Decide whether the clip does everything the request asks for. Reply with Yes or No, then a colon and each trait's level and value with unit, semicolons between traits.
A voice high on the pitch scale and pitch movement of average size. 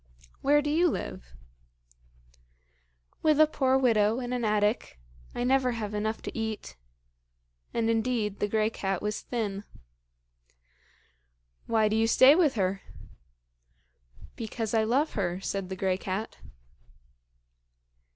Yes: high, 220 Hz; average, 3.5 semitones